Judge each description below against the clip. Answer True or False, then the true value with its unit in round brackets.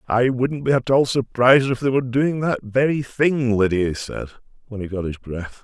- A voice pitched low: True (125 Hz)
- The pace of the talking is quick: True (225 wpm)